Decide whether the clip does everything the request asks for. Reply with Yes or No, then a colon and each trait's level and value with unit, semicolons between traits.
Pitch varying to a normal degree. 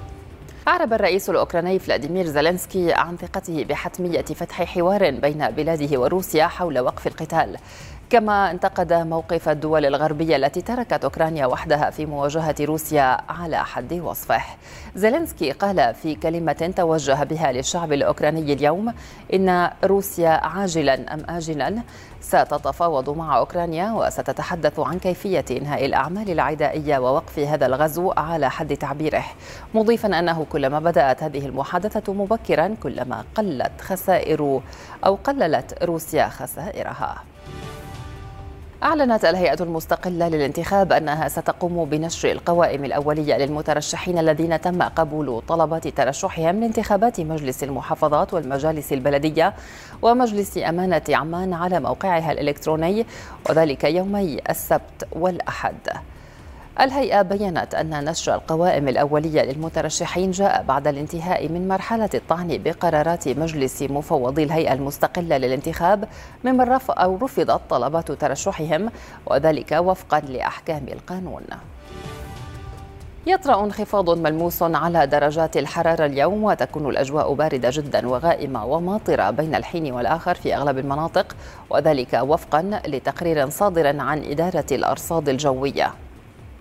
Yes: average, 3.8 semitones